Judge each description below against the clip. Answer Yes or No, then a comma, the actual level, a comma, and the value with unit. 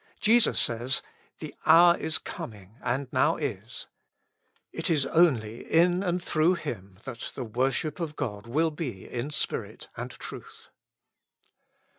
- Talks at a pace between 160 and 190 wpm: No, slow, 135 wpm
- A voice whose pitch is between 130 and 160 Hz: Yes, medium, 140 Hz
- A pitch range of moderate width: No, wide, 6.1 semitones